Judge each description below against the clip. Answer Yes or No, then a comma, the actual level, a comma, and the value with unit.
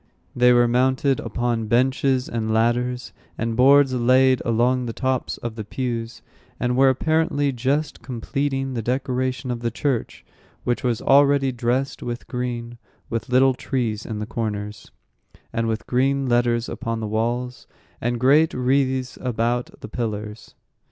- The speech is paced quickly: No, average, 145 wpm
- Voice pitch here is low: Yes, low, 125 Hz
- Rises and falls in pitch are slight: Yes, narrow, 2.1 semitones